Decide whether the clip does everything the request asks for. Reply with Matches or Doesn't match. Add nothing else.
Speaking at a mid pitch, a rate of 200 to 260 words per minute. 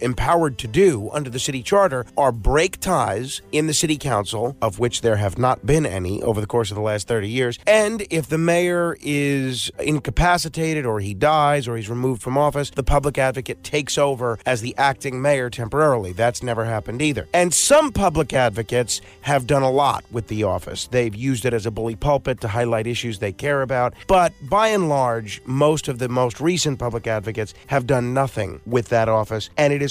Doesn't match